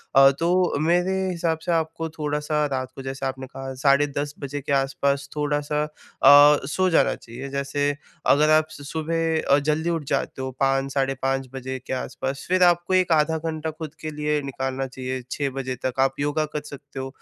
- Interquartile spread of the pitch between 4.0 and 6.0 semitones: No, average, 2.7 semitones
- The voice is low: No, medium, 145 Hz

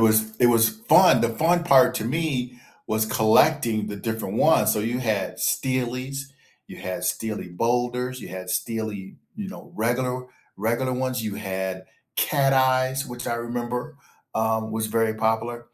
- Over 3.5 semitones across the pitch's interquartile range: No, average, 2.8 semitones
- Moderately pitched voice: No, low, 120 Hz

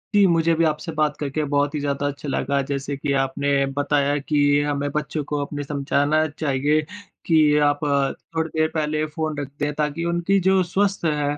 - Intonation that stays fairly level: Yes, narrow, 1.6 semitones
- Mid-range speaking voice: Yes, medium, 150 Hz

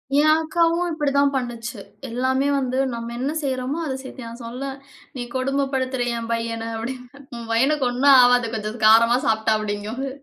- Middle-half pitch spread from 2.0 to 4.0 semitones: Yes, average, 3.1 semitones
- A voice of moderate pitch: No, very high, 255 Hz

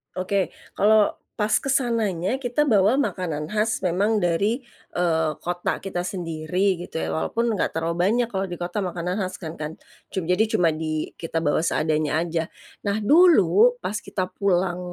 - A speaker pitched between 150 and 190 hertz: Yes, medium, 185 Hz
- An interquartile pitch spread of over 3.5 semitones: Yes, average, 4.0 semitones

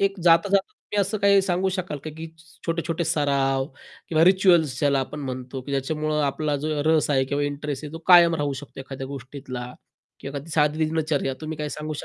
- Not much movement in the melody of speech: No, average, 3.0 semitones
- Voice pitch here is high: No, medium, 150 Hz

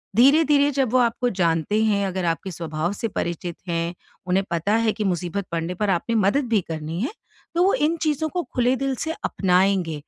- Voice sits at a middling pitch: No, high, 200 Hz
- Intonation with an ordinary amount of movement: No, wide, 7.2 semitones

